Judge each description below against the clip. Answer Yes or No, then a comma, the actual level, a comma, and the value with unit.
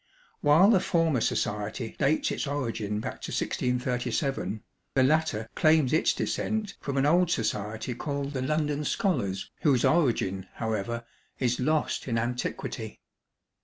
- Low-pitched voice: Yes, low, 130 Hz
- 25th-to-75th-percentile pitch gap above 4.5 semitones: Yes, average, 5.1 semitones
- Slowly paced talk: Yes, slow, 130 wpm